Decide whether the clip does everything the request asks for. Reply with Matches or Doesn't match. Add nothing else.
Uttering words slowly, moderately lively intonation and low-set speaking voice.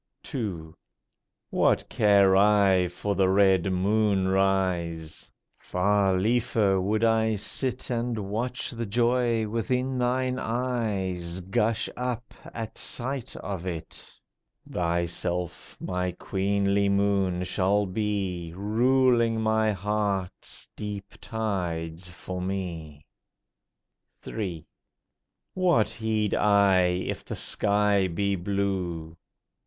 Matches